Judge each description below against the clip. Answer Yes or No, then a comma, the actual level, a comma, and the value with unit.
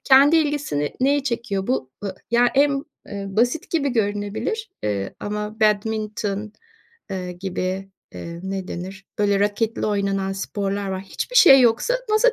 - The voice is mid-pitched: No, high, 210 Hz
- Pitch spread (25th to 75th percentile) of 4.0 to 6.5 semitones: Yes, average, 4.9 semitones